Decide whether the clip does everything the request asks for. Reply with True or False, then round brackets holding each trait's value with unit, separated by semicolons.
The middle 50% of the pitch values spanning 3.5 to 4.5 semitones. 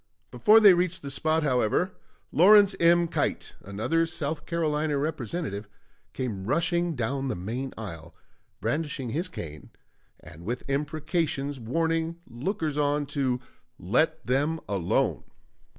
False (5.0 semitones)